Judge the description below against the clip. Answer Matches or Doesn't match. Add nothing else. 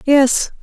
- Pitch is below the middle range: Doesn't match